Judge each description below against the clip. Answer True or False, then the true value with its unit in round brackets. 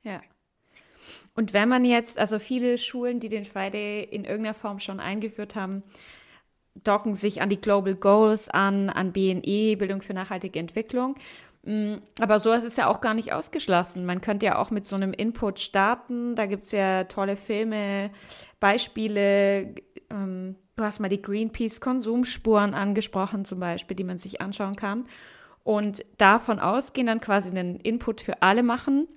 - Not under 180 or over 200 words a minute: False (160 wpm)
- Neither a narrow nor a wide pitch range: False (2.3 semitones)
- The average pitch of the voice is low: False (210 Hz)